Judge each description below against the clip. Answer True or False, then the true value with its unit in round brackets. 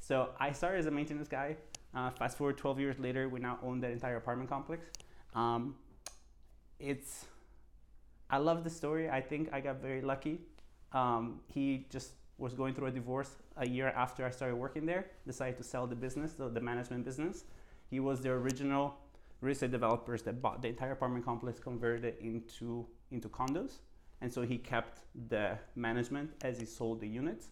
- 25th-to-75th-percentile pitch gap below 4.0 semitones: True (2.4 semitones)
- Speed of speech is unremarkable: True (185 wpm)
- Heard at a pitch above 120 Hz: True (130 Hz)